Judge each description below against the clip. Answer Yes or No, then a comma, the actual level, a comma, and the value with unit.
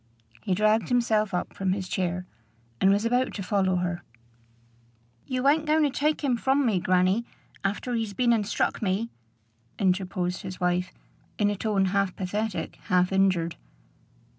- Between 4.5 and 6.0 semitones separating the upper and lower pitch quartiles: No, average, 4.0 semitones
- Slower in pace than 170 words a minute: Yes, average, 160 wpm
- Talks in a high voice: Yes, high, 200 Hz